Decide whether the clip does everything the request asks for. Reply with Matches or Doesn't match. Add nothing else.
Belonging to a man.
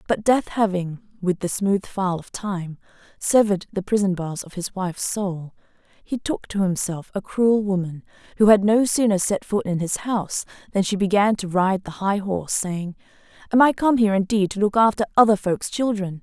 Doesn't match